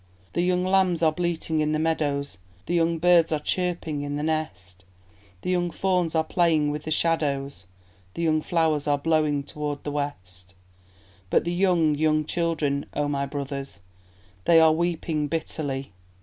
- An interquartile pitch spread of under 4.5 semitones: Yes, average, 2.7 semitones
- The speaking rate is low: No, average, 165 wpm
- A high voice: No, medium, 155 Hz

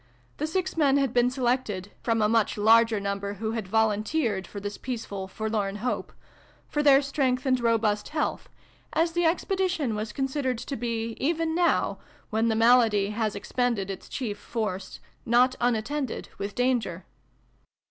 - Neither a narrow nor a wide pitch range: Yes, average, 4.3 semitones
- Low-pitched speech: No, high, 230 Hz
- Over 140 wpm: Yes, average, 160 wpm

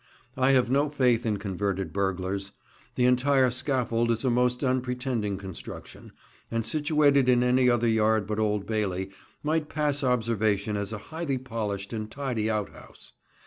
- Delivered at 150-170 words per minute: Yes, average, 155 wpm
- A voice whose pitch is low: Yes, low, 115 Hz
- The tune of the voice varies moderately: Yes, average, 3.9 semitones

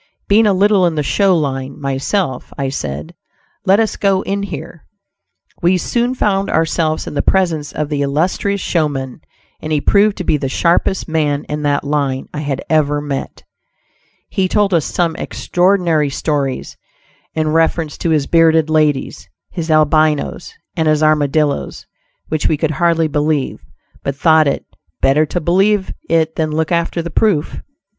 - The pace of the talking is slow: No, average, 160 wpm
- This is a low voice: No, medium, 155 Hz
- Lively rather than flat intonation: No, average, 3.2 semitones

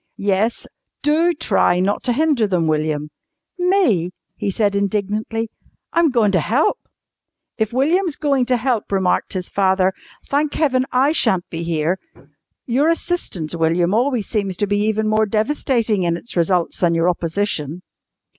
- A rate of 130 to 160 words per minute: Yes, average, 150 wpm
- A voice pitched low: No, high, 210 Hz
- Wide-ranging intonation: Yes, wide, 6.3 semitones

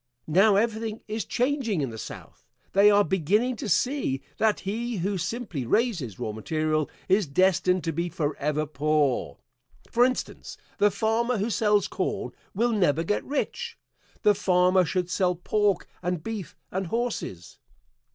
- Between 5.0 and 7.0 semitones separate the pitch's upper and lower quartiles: Yes, wide, 5.6 semitones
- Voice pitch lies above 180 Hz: Yes, high, 190 Hz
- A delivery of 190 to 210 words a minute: No, average, 150 wpm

